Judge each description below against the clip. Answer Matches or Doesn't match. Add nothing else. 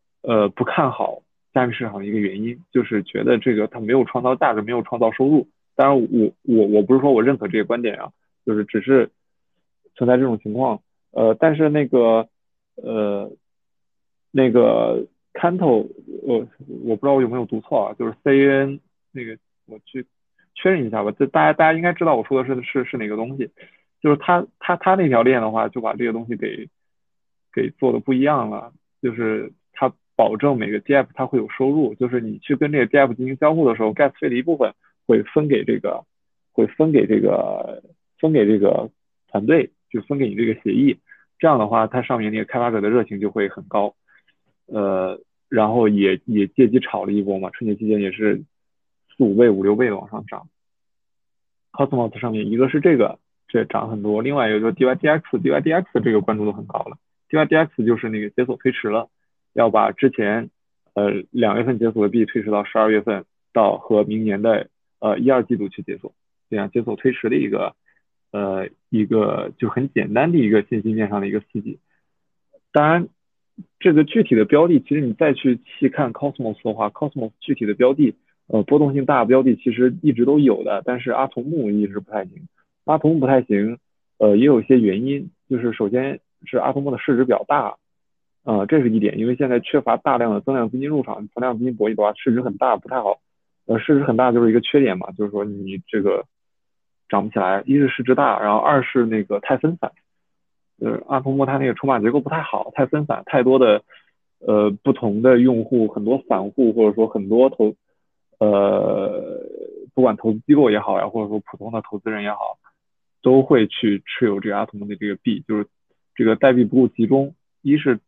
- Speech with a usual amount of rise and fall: Matches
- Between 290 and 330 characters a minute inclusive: Matches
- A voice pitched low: Matches